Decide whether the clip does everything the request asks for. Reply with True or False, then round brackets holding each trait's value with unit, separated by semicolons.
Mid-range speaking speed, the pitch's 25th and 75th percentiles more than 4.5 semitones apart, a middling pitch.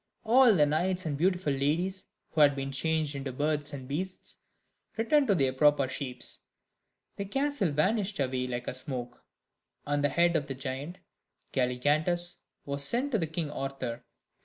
True (155 wpm; 5.1 semitones; 150 Hz)